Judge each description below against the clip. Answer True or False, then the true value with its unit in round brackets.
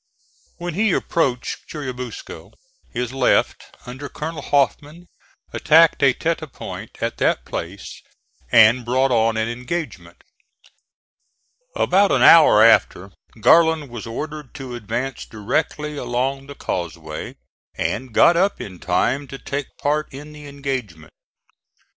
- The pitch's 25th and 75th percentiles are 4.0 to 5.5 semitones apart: True (4.5 semitones)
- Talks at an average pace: False (125 wpm)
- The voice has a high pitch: False (135 Hz)